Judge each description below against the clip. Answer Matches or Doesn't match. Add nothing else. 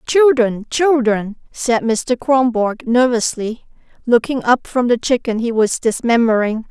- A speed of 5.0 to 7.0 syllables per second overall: Doesn't match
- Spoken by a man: Doesn't match